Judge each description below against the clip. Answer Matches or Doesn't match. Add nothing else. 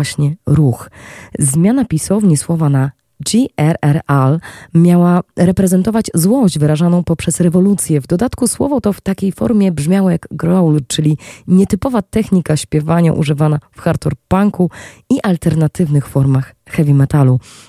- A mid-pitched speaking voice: Matches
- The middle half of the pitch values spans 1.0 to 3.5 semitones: Doesn't match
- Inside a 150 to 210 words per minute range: Doesn't match